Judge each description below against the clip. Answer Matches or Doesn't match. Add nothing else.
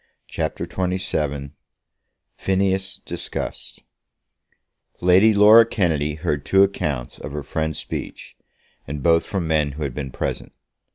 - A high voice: Doesn't match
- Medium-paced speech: Doesn't match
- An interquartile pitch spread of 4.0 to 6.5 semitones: Matches